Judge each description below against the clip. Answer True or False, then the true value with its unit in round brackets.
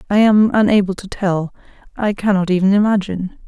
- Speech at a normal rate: True (155 wpm)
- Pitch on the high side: True (200 Hz)